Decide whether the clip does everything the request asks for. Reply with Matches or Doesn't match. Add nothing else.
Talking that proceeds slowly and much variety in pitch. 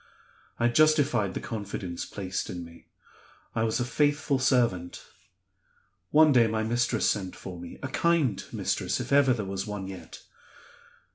Doesn't match